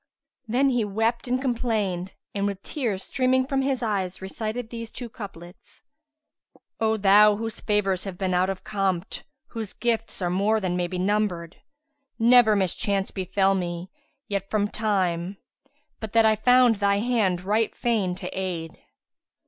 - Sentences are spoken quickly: No, average, 160 wpm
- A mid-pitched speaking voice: No, high, 205 Hz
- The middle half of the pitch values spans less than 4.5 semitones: Yes, average, 3.4 semitones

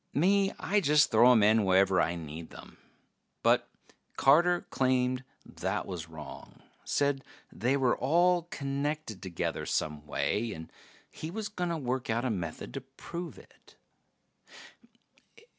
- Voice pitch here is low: Yes, low, 130 Hz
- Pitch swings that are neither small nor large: No, wide, 8.1 semitones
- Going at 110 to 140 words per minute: Yes, slow, 135 wpm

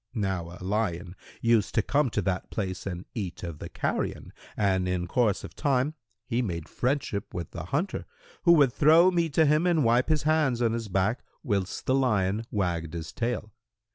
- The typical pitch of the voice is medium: No, low, 110 Hz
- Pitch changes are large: Yes, wide, 6.6 semitones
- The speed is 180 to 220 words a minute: Yes, average, 190 wpm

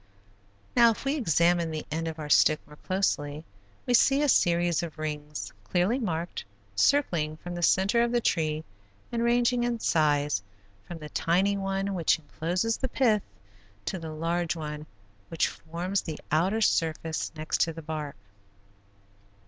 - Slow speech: No, average, 155 wpm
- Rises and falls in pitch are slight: No, average, 4.5 semitones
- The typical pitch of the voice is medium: Yes, medium, 170 Hz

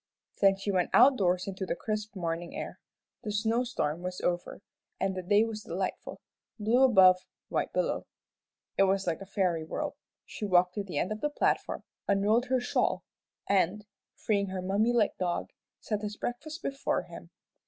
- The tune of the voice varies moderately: Yes, average, 3.0 semitones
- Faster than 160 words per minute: Yes, average, 175 wpm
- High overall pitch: Yes, high, 200 Hz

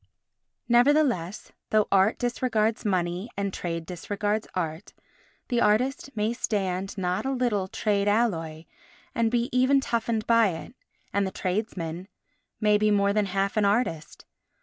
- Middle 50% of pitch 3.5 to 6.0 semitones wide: Yes, average, 3.8 semitones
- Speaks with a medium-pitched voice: No, high, 210 Hz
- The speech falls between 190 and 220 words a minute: No, average, 140 wpm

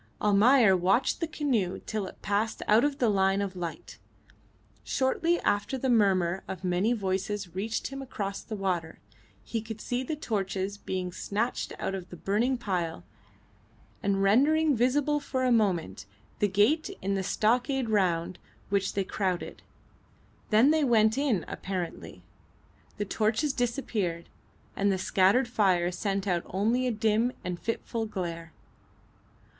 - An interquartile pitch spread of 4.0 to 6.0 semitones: Yes, average, 4.5 semitones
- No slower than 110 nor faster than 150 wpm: Yes, average, 145 wpm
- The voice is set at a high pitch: Yes, high, 205 Hz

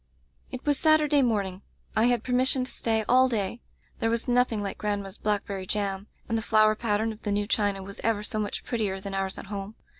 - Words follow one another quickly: Yes, fast, 215 wpm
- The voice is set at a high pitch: Yes, high, 215 Hz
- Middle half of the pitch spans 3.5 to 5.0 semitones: No, average, 3.1 semitones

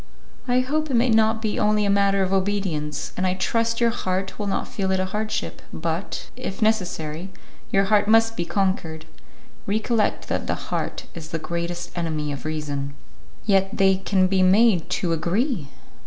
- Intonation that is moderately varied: Yes, average, 4.2 semitones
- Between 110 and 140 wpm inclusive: No, average, 175 wpm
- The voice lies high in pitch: Yes, high, 195 Hz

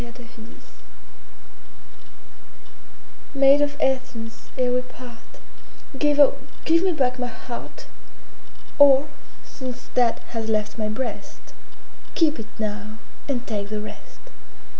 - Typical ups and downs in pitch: Yes, average, 3.7 semitones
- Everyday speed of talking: No, slow, 110 wpm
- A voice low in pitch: No, very high, 250 Hz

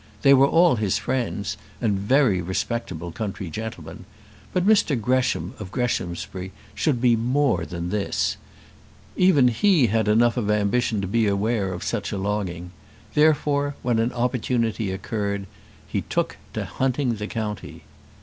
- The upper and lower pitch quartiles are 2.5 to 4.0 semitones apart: No, average, 4.4 semitones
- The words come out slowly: No, average, 145 wpm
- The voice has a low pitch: Yes, low, 110 Hz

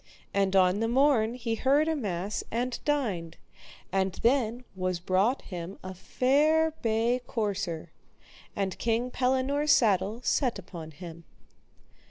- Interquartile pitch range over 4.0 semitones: Yes, average, 5.2 semitones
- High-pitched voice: Yes, high, 220 Hz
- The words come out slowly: Yes, slow, 130 wpm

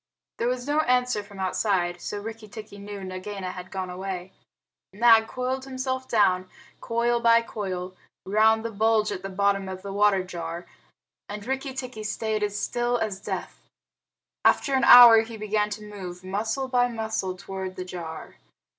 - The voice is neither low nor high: No, high, 210 Hz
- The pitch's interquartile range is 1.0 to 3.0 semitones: No, average, 3.6 semitones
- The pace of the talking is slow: No, average, 165 wpm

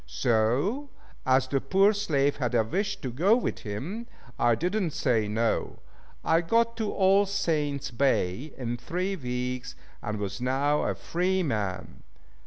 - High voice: No, medium, 140 Hz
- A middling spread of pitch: No, wide, 7.8 semitones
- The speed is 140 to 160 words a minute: Yes, average, 155 wpm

